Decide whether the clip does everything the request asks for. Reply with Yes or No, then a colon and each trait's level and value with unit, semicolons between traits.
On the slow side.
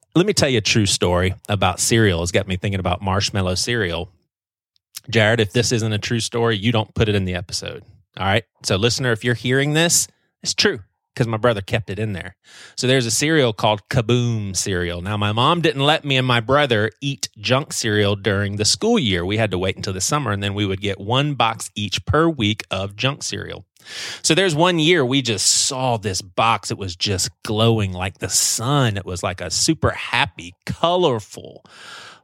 No: fast, 210 wpm